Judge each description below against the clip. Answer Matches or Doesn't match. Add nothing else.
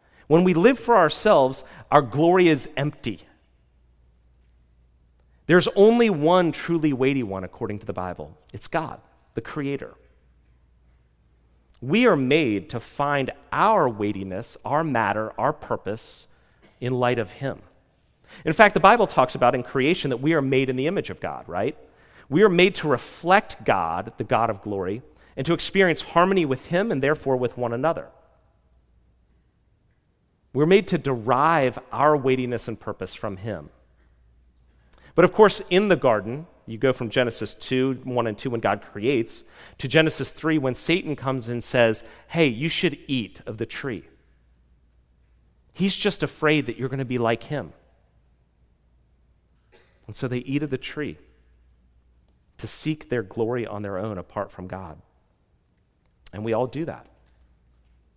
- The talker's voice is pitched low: Matches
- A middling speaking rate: Matches